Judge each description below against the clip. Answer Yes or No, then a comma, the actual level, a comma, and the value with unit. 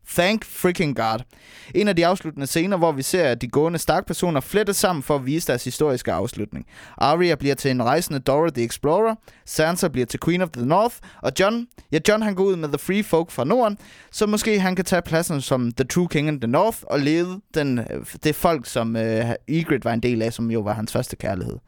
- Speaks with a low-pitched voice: No, medium, 155 Hz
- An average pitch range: No, wide, 6.0 semitones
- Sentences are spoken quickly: Yes, fast, 230 wpm